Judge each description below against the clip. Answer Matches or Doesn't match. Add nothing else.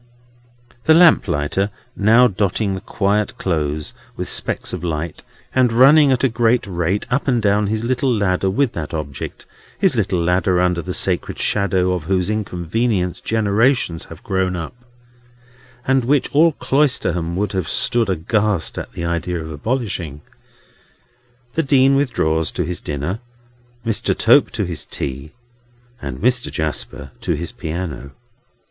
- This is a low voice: Matches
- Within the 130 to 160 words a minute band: Matches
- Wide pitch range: Matches